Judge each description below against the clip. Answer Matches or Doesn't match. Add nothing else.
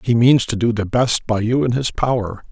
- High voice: Doesn't match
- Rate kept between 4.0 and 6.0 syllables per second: Matches